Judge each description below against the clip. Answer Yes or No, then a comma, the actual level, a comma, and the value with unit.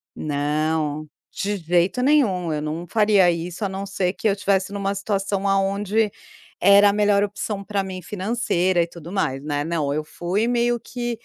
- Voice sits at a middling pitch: No, high, 195 Hz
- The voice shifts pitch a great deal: No, average, 3.4 semitones